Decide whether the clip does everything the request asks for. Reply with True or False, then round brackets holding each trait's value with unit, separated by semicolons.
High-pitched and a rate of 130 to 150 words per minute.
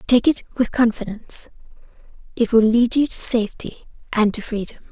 True (230 Hz; 145 wpm)